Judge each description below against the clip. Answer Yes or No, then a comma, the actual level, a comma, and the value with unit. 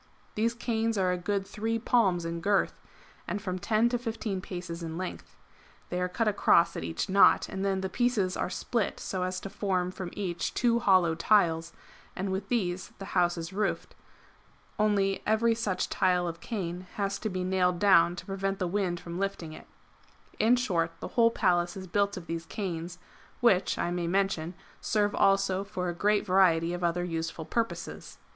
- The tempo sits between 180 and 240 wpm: Yes, average, 190 wpm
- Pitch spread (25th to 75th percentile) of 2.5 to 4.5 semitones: Yes, average, 2.8 semitones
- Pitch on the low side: No, high, 190 Hz